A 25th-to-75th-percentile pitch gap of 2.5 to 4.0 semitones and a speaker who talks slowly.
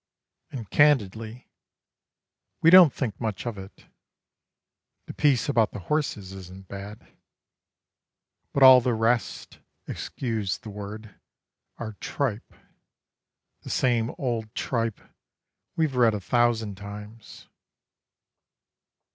Yes: average, 3.5 semitones; slow, 105 wpm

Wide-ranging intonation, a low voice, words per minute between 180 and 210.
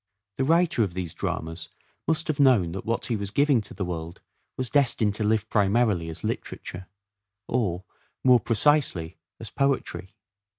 No: wide, 6.4 semitones; low, 110 Hz; average, 160 wpm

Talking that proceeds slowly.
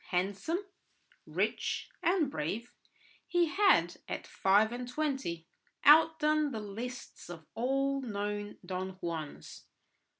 Yes: slow, 105 wpm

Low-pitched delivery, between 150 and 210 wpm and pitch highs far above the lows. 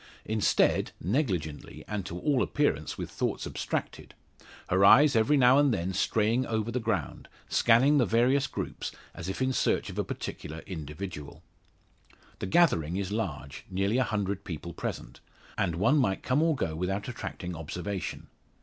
Yes: low, 100 Hz; average, 160 wpm; wide, 6.3 semitones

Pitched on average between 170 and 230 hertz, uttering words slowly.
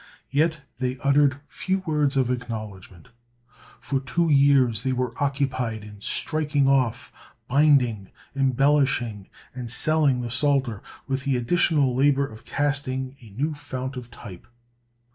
No: low, 130 Hz; slow, 130 wpm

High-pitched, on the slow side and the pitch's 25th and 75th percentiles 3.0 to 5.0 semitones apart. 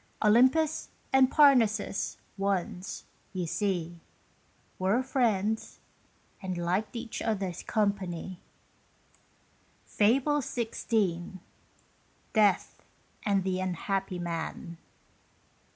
Yes: high, 200 Hz; slow, 75 wpm; average, 3.9 semitones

